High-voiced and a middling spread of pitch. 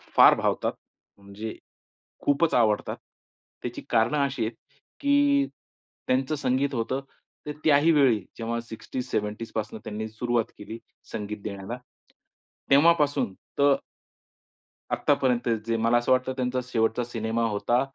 No: low, 120 Hz; average, 3.6 semitones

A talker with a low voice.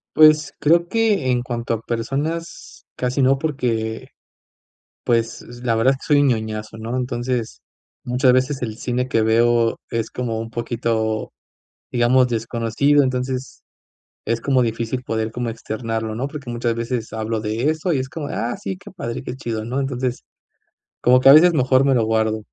Yes: low, 120 Hz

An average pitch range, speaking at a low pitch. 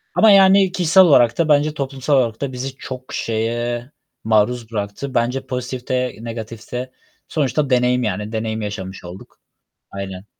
Yes: average, 3.7 semitones; low, 125 Hz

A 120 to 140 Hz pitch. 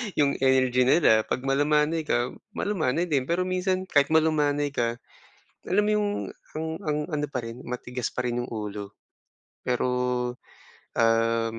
Yes: low, 135 Hz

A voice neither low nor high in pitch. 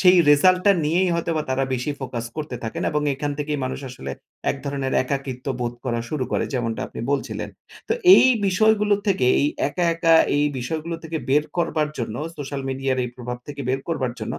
Yes: medium, 145 Hz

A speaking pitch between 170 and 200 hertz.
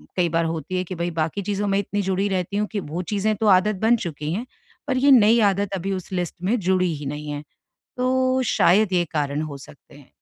Yes: medium, 185 Hz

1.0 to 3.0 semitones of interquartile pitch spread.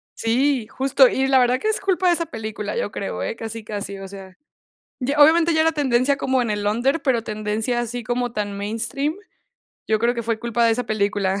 No: average, 4.3 semitones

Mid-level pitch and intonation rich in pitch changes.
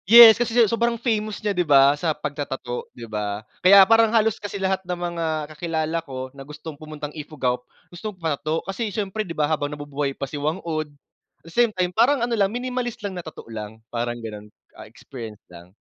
Yes: medium, 160 Hz; wide, 6.7 semitones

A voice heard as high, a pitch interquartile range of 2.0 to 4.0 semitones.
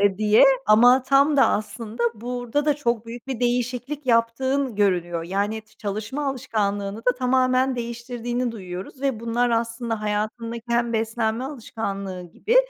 Yes: high, 235 Hz; average, 2.9 semitones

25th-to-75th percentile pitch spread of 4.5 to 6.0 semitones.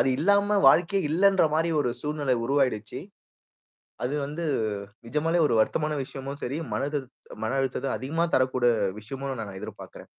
No: average, 4.0 semitones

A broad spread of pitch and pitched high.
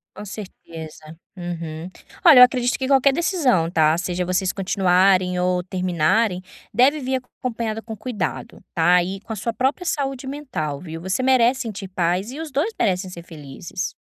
Yes: wide, 6.1 semitones; high, 195 Hz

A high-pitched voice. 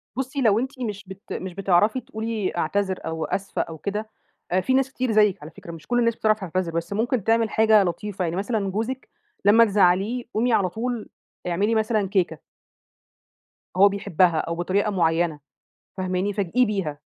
Yes: high, 200 Hz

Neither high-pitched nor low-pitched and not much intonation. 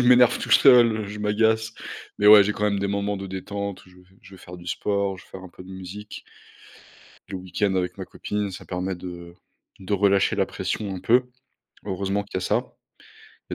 No: low, 100 Hz; narrow, 2.0 semitones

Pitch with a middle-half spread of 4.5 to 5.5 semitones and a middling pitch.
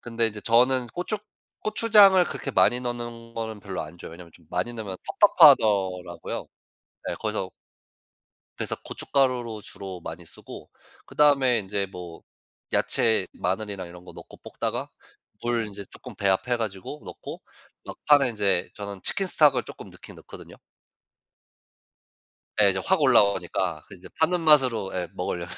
No: average, 5.2 semitones; low, 110 Hz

